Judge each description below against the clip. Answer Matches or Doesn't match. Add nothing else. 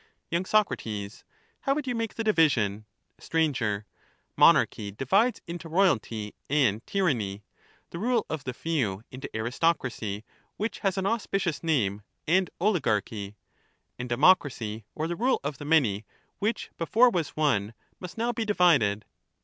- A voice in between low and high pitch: Matches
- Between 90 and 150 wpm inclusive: Matches